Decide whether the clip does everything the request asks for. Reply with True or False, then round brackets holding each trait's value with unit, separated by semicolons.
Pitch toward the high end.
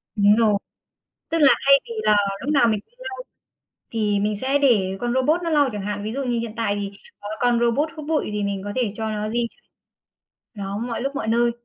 True (235 Hz)